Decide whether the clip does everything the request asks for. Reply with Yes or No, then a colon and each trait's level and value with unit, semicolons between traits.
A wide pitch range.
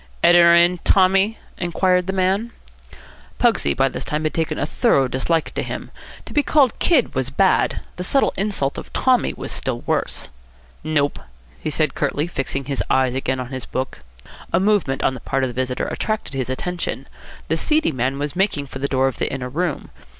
Yes: wide, 5.9 semitones